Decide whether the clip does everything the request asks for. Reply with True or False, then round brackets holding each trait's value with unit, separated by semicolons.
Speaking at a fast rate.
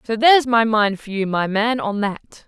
True (240 wpm)